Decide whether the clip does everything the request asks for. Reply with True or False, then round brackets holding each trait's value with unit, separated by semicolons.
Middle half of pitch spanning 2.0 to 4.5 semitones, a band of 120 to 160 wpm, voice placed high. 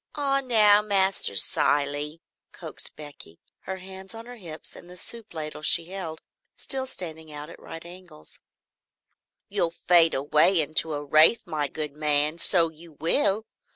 False (4.1 semitones; 155 wpm; 165 Hz)